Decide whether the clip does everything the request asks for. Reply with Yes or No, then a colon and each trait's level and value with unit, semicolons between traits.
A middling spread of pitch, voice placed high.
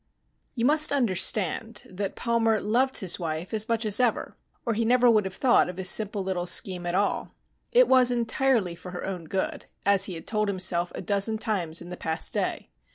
Yes: average, 4.2 semitones; high, 205 Hz